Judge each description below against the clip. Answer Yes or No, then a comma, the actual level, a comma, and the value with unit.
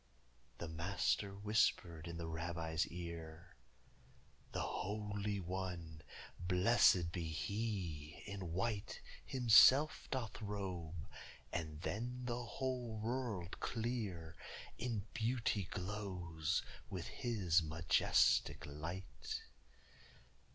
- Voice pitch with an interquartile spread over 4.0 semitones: Yes, average, 4.8 semitones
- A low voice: Yes, very low, 95 Hz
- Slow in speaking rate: Yes, slow, 90 wpm